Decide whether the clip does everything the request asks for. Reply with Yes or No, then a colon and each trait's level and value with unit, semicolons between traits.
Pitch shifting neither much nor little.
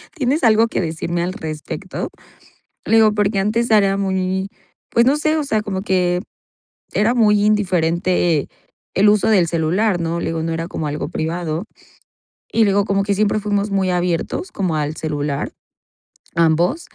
Yes: average, 4.1 semitones